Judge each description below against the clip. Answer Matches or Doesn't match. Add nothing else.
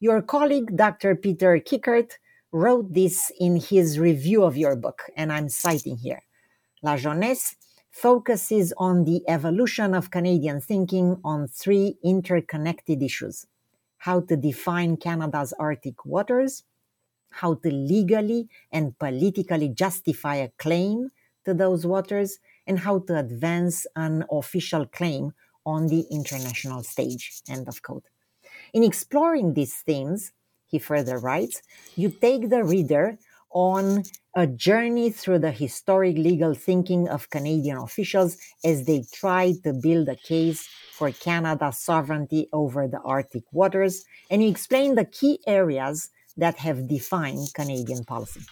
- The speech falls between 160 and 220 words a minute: Doesn't match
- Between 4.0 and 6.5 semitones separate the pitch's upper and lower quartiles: Matches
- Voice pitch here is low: Doesn't match